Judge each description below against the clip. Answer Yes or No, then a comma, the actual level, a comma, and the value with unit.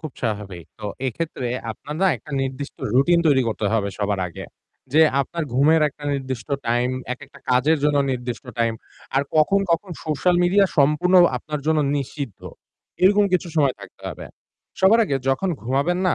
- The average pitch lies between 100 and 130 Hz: No, medium, 140 Hz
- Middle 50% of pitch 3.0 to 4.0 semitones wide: No, average, 4.8 semitones